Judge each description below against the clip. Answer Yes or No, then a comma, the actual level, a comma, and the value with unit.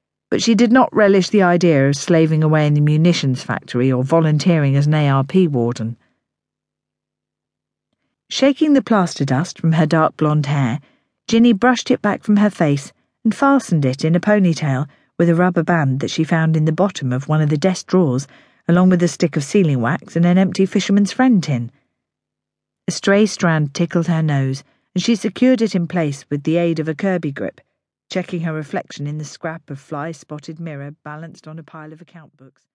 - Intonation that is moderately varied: Yes, average, 4.2 semitones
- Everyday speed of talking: Yes, average, 195 wpm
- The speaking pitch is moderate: Yes, medium, 165 Hz